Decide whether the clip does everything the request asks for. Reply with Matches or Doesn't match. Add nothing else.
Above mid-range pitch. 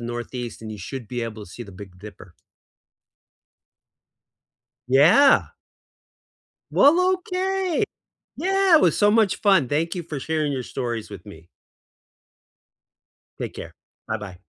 Doesn't match